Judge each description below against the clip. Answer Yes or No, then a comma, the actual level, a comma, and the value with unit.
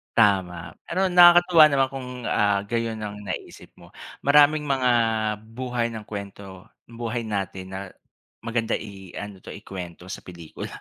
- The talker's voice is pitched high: No, low, 110 Hz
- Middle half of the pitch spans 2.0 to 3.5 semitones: No, average, 4.7 semitones